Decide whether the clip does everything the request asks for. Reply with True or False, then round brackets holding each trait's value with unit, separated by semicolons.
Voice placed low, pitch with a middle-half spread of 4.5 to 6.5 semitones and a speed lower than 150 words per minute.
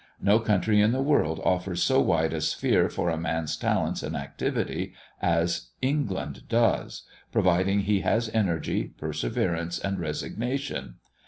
True (95 Hz; 4.9 semitones; 140 wpm)